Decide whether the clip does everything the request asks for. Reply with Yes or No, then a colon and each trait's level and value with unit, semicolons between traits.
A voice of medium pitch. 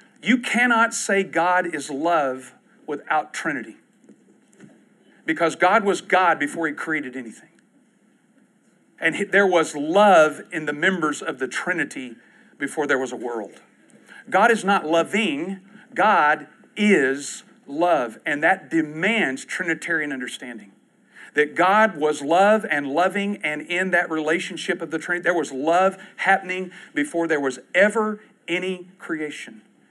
Yes: medium, 180 Hz